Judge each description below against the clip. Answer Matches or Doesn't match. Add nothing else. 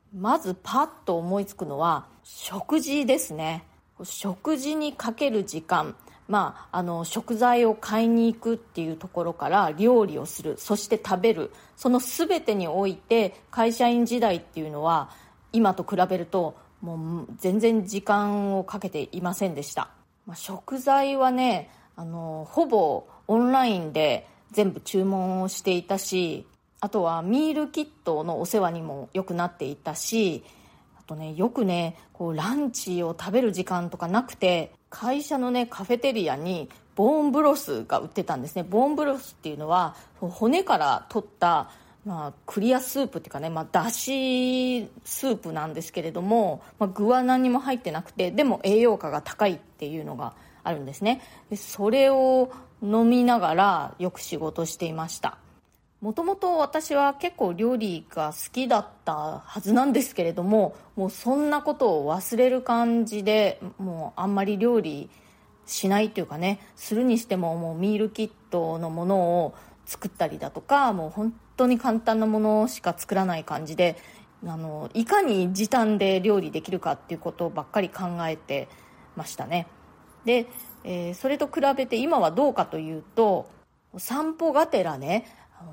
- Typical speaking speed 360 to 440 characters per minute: Doesn't match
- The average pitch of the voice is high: Matches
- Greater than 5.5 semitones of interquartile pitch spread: Matches